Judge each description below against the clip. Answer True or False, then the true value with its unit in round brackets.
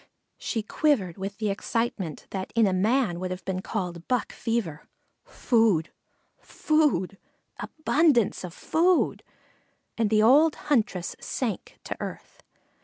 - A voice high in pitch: True (215 Hz)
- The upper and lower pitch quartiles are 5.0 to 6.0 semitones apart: True (5.4 semitones)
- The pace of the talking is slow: True (125 wpm)